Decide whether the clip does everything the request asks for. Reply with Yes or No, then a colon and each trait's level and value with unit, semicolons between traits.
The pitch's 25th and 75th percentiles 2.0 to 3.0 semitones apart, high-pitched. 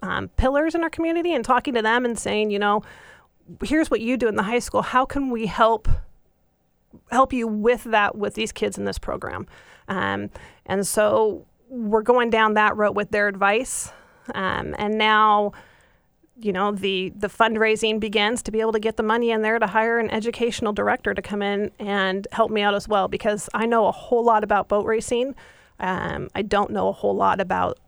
Yes: narrow, 2.4 semitones; high, 220 Hz